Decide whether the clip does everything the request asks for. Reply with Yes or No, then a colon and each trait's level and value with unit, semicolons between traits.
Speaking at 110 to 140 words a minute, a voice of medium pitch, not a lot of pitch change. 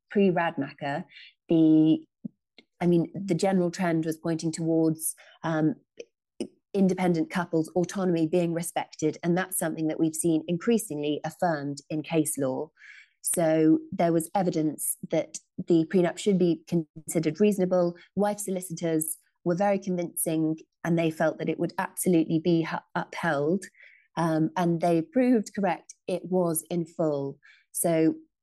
Yes: slow, 135 wpm; medium, 170 Hz; narrow, 2.2 semitones